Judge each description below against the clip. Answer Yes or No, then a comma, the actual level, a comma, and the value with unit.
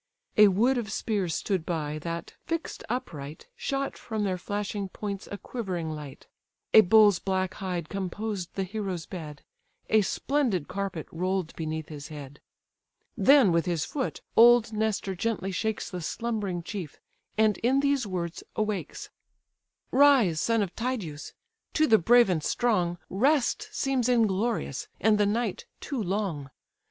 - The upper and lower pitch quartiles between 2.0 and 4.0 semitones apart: No, average, 4.8 semitones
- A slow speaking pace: No, average, 145 wpm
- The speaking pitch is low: No, high, 200 Hz